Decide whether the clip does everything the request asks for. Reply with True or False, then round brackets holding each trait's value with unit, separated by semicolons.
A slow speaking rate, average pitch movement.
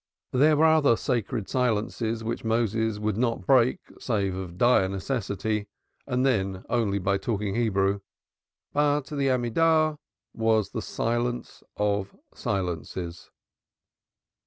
True (115 wpm; 4.2 semitones)